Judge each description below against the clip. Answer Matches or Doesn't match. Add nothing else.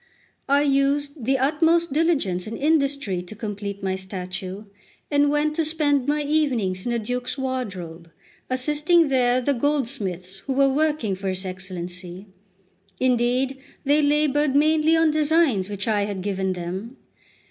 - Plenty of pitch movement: Matches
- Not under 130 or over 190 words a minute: Matches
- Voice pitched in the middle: Doesn't match